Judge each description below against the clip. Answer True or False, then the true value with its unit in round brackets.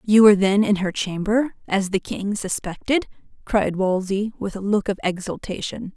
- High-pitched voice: True (200 Hz)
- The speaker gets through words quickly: False (170 wpm)